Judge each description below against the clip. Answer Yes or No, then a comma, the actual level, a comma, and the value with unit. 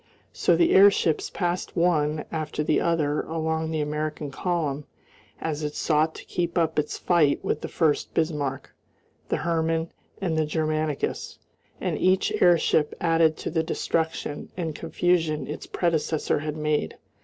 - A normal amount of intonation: No, narrow, 1.7 semitones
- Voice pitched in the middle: Yes, medium, 160 Hz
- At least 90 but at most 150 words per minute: Yes, average, 145 wpm